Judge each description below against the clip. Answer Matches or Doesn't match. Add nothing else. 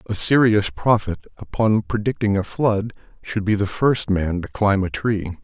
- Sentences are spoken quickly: Doesn't match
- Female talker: Doesn't match